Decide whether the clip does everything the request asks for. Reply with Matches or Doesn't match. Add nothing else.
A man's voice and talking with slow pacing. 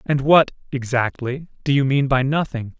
Matches